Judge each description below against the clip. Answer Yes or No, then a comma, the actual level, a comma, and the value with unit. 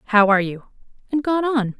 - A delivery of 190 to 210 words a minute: Yes, average, 200 wpm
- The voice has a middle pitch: No, high, 235 Hz